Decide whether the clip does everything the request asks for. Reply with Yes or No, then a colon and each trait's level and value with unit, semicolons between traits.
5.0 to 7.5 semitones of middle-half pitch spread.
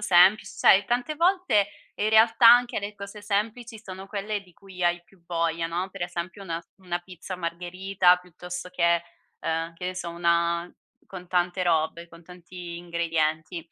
No: average, 2.7 semitones